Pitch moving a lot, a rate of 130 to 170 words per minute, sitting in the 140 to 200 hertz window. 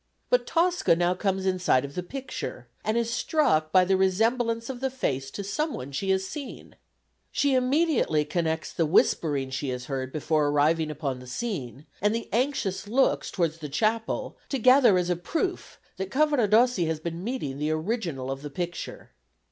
No: wide, 7.8 semitones; average, 180 wpm; medium, 185 Hz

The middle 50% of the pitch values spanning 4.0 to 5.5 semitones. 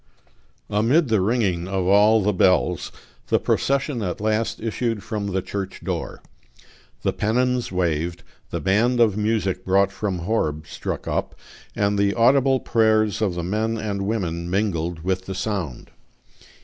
No: average, 3.3 semitones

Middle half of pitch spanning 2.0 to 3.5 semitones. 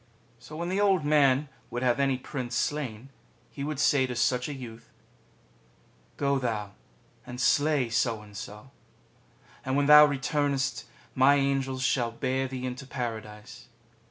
Yes: average, 2.8 semitones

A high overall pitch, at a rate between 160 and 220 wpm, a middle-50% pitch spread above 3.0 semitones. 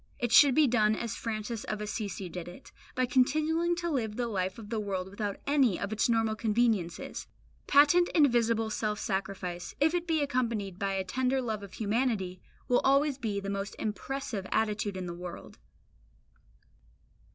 Yes: high, 220 Hz; average, 175 wpm; average, 4.5 semitones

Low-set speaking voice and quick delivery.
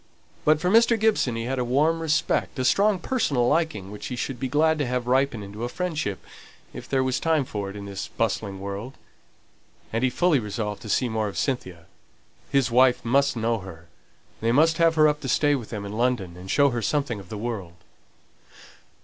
Yes: low, 125 Hz; fast, 210 wpm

